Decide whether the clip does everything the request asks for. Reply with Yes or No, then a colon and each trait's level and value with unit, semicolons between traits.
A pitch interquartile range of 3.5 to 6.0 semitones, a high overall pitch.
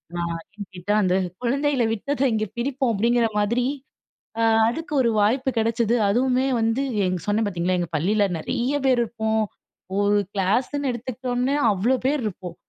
Yes: average, 4.0 semitones; high, 230 Hz